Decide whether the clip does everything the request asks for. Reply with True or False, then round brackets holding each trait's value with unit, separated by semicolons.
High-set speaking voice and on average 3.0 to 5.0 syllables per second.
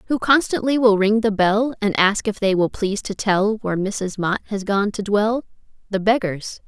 True (210 Hz; 4.8 syllables/s)